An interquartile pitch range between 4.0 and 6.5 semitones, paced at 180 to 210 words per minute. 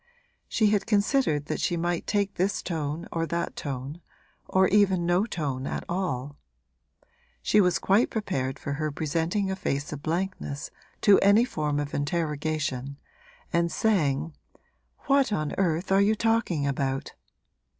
No: average, 5.3 semitones; average, 145 wpm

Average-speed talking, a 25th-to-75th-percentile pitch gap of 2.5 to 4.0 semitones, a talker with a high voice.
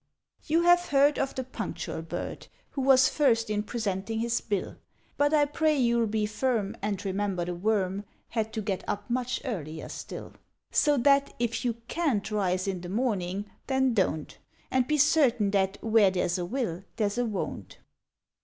No: average, 175 wpm; average, 4.9 semitones; high, 220 Hz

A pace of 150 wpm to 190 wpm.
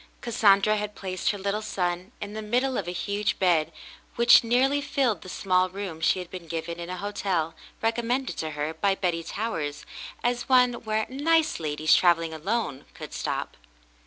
Yes: average, 175 wpm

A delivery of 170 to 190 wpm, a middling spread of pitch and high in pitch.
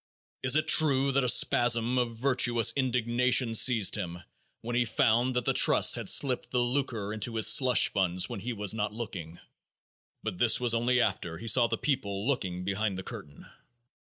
No: average, 185 wpm; average, 3.3 semitones; low, 115 Hz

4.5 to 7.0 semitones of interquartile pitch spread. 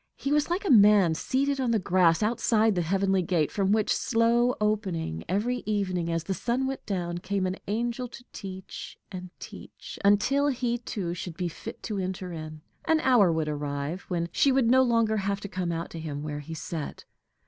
Yes: wide, 5.5 semitones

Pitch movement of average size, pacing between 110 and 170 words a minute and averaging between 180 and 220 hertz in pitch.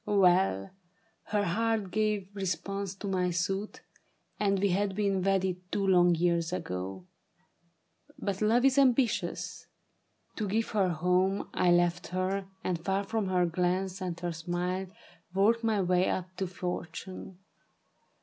No: narrow, 2.2 semitones; average, 150 wpm; high, 190 Hz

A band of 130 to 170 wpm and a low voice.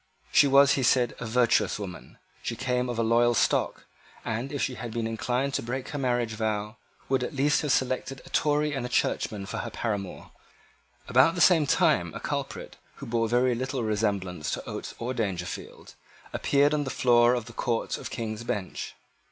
No: average, 195 wpm; low, 120 Hz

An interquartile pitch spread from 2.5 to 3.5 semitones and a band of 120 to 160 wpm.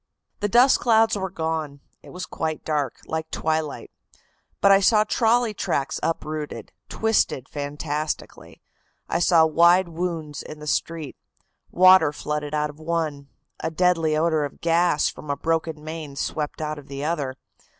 Yes: average, 2.8 semitones; average, 150 wpm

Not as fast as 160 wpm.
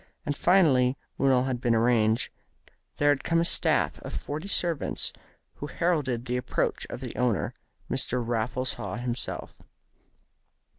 Yes: average, 145 wpm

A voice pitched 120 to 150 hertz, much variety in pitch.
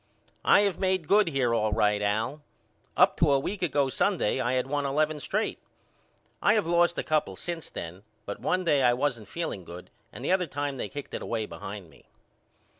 Yes: medium, 140 Hz; wide, 7.3 semitones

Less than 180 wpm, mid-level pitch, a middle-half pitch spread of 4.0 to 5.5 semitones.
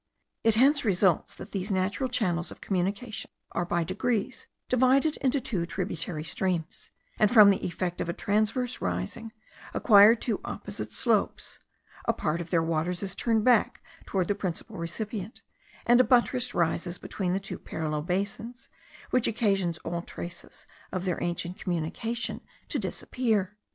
No: average, 150 wpm; high, 195 Hz; average, 4.7 semitones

